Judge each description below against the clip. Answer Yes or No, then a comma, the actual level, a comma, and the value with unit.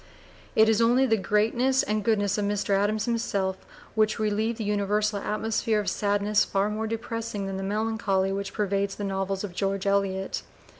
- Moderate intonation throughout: No, narrow, 1.9 semitones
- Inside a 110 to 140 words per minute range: No, average, 170 wpm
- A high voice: Yes, high, 210 Hz